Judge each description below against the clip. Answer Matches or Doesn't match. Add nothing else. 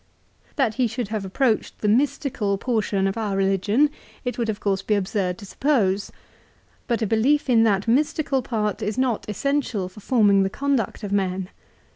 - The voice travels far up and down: Doesn't match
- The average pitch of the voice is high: Matches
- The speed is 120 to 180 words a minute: Matches